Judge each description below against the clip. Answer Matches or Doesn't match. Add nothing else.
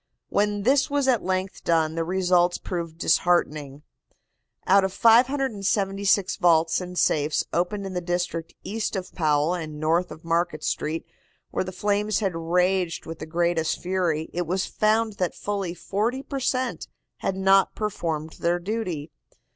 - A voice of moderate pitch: Matches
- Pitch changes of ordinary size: Matches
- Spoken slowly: Doesn't match